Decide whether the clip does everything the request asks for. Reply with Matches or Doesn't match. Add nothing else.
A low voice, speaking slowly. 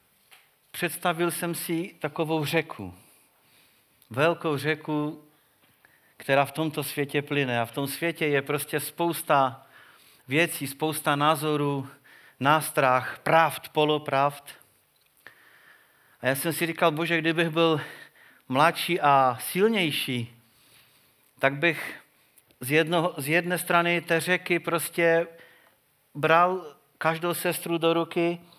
Doesn't match